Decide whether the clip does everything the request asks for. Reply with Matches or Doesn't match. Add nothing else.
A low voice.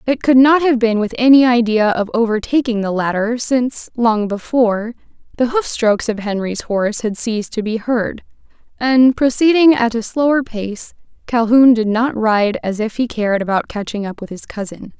Doesn't match